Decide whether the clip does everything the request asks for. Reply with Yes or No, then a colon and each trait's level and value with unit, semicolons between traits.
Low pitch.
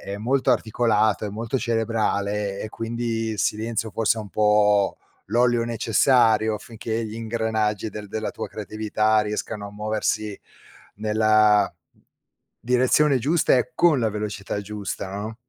Yes: low, 110 Hz